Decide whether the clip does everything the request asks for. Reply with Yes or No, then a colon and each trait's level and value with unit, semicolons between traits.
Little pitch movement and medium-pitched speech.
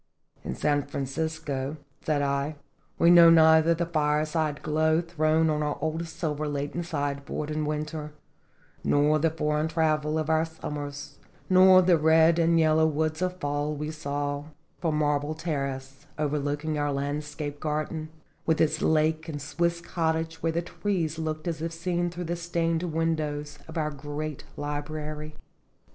Yes: narrow, 1.6 semitones; medium, 155 Hz